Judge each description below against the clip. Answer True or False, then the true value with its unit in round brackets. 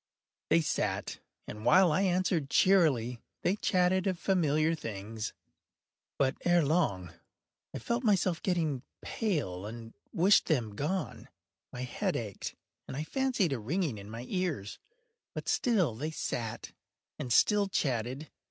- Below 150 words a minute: True (135 wpm)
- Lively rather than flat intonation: True (7.9 semitones)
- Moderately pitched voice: True (155 Hz)